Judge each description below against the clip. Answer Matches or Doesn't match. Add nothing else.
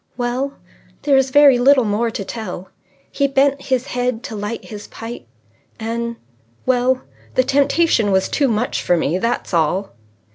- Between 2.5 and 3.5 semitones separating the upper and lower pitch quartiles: Doesn't match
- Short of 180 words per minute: Matches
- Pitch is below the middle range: Doesn't match